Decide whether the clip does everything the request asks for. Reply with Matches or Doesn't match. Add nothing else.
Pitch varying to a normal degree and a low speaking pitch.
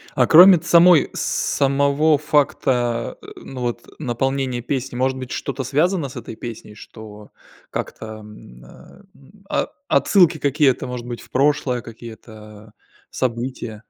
Matches